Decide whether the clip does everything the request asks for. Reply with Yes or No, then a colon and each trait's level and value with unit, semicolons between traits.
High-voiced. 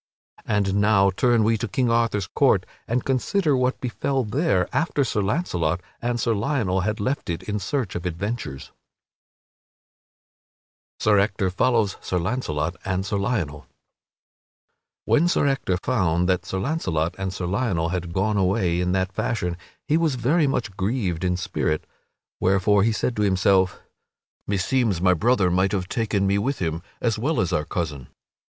No: low, 100 Hz